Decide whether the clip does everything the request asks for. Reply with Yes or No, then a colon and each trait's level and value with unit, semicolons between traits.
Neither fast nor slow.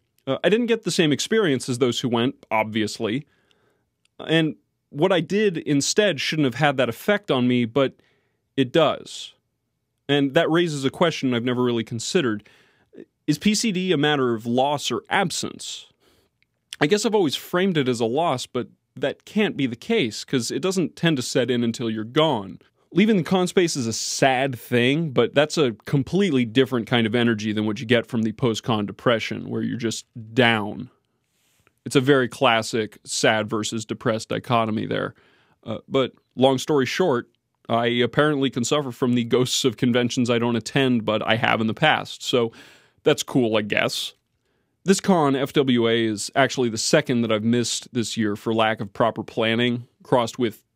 Yes: average, 180 wpm